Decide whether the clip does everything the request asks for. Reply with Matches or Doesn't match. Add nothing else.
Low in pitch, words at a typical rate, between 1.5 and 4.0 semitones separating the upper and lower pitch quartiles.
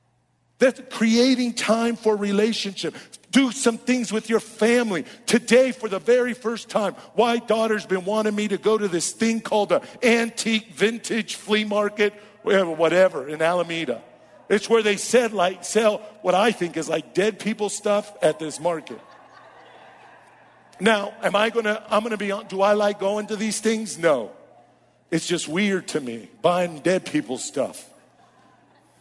Doesn't match